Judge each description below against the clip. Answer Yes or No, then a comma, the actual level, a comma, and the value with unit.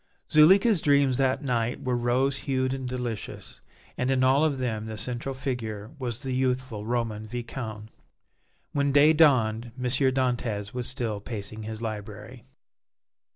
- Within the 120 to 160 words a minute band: Yes, average, 145 wpm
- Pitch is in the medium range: No, low, 125 Hz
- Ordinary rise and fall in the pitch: Yes, average, 3.1 semitones